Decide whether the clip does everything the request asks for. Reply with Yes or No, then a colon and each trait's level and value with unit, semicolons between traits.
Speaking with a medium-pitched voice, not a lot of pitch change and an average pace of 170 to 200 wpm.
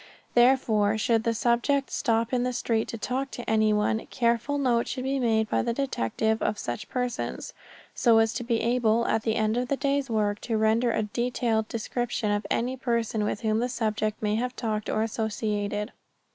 No: high, 230 Hz; narrow, 2.2 semitones; average, 190 wpm